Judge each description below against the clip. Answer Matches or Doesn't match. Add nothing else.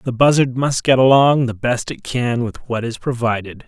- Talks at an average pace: Doesn't match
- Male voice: Matches